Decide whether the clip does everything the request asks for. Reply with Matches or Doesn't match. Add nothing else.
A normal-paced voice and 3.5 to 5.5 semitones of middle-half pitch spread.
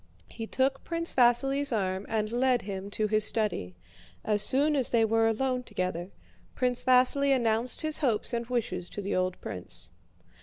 Matches